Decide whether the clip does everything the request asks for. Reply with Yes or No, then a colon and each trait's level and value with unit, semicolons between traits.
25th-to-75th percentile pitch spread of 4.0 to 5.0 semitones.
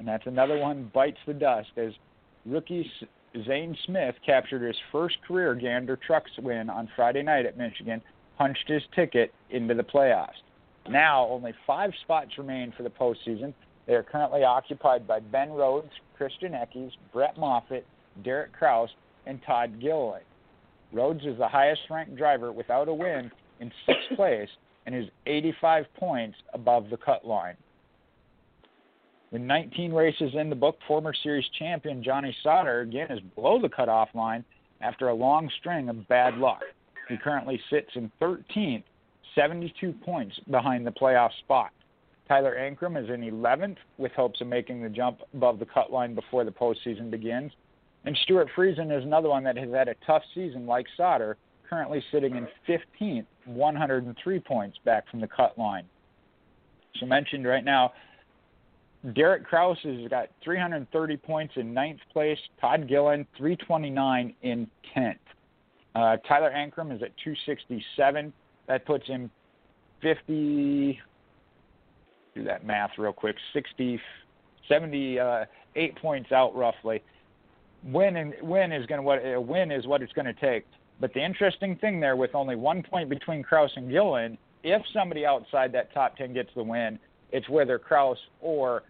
Yes: average, 4.4 semitones